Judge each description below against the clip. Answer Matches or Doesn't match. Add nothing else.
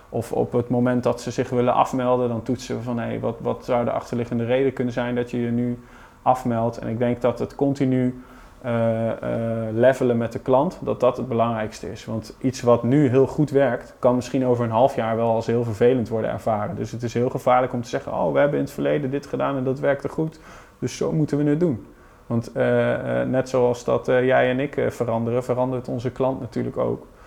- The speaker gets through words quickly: Matches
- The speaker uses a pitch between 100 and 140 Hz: Matches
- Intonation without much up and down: Matches